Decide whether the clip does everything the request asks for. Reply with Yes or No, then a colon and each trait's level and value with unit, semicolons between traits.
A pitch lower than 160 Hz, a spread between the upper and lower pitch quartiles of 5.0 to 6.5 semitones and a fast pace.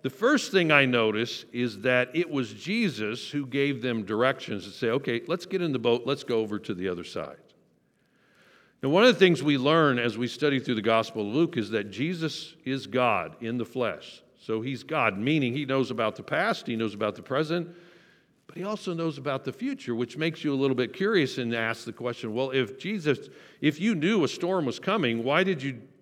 Yes: low, 135 Hz; wide, 5.5 semitones; fast, 225 wpm